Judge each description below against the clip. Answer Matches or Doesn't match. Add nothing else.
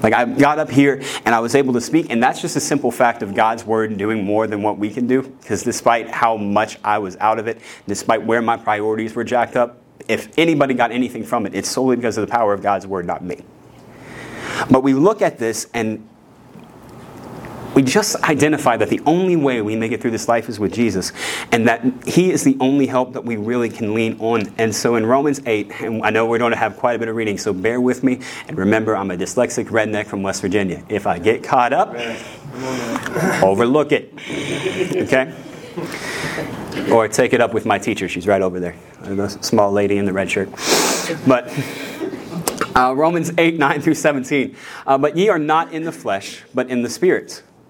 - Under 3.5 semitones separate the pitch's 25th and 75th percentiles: Doesn't match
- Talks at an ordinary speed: Doesn't match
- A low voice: Matches